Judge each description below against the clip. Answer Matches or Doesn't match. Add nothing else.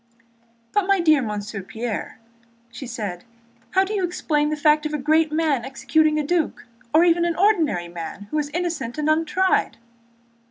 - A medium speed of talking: Matches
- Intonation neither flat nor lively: Doesn't match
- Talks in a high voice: Matches